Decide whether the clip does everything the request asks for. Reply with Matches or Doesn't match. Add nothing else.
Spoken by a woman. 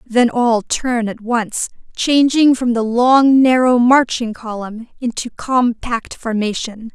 Matches